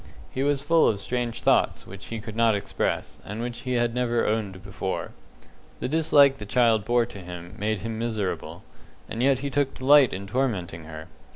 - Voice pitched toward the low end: Yes, low, 115 Hz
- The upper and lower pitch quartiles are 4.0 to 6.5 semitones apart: Yes, average, 4.3 semitones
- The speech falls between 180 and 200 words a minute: Yes, average, 190 wpm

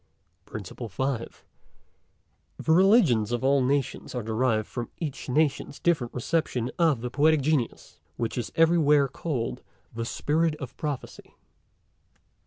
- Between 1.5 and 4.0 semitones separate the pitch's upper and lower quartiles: No, average, 4.6 semitones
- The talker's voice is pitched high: No, low, 135 Hz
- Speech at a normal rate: No, slow, 125 wpm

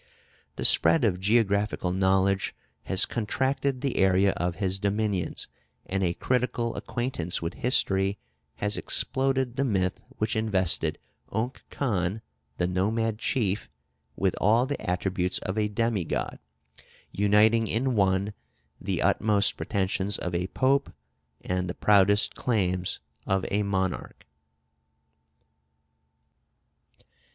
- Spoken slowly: Yes, slow, 115 wpm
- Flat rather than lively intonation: No, average, 3.3 semitones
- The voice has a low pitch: Yes, low, 100 Hz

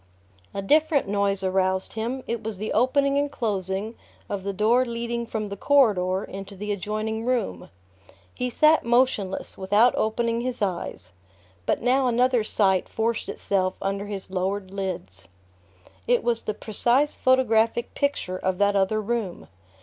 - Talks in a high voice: Yes, high, 215 Hz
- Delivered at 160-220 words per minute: No, average, 150 wpm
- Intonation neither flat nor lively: Yes, average, 3.7 semitones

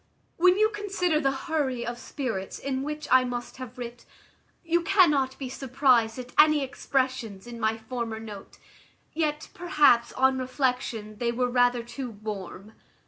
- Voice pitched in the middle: No, very high, 255 Hz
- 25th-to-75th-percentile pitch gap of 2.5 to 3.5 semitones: No, average, 3.9 semitones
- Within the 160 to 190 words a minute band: No, average, 150 wpm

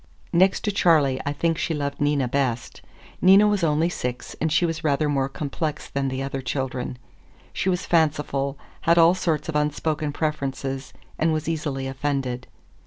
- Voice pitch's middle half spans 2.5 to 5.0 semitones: Yes, average, 3.3 semitones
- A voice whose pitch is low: No, medium, 150 Hz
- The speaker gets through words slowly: No, average, 170 wpm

